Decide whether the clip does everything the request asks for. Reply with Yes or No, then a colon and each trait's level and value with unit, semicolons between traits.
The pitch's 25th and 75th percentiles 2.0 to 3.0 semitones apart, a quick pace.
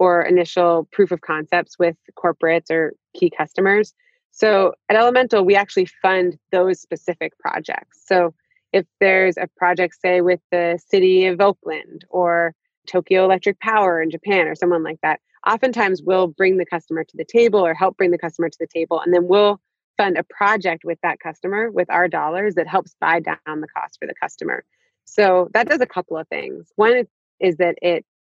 No: narrow, 2.5 semitones; average, 185 wpm